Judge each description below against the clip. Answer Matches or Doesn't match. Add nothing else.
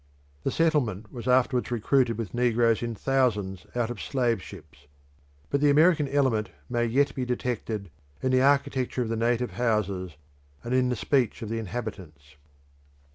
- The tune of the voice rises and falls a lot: Doesn't match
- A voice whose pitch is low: Matches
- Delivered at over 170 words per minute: Doesn't match